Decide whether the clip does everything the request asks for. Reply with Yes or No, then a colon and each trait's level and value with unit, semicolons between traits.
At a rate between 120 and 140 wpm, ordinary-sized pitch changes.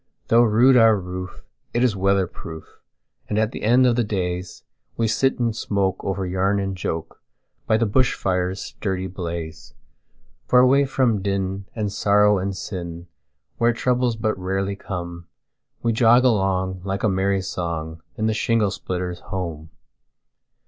Yes: slow, 135 wpm; average, 3.4 semitones